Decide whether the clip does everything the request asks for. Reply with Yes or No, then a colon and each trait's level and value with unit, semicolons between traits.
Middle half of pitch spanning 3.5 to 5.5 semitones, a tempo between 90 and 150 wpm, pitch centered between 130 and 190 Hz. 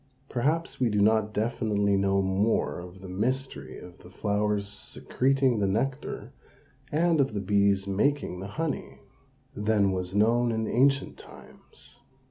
No: average, 4.5 semitones; average, 140 wpm; low, 105 Hz